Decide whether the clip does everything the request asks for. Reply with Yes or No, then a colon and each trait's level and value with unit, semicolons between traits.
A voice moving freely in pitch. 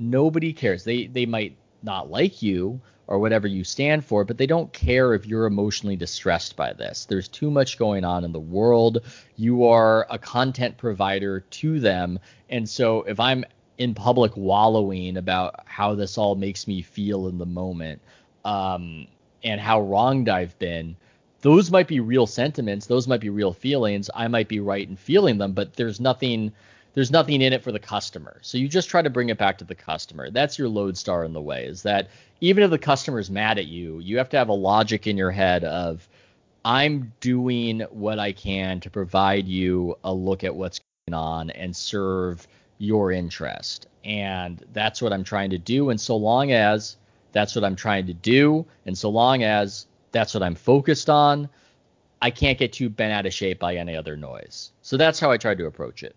No: average, 4.5 semitones